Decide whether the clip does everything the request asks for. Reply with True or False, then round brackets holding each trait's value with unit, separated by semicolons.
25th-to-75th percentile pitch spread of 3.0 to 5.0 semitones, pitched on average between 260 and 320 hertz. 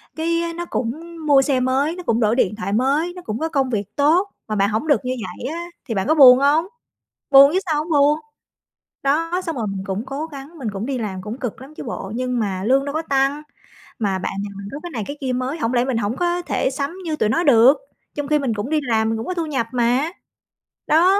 False (5.4 semitones; 270 Hz)